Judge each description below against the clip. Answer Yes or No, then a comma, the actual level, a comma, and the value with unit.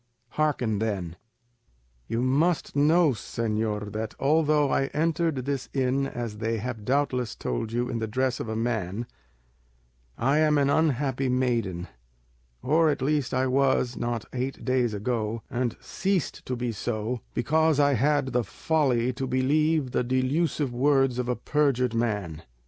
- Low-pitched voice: Yes, low, 130 Hz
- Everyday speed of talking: Yes, average, 155 wpm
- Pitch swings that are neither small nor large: Yes, average, 3.6 semitones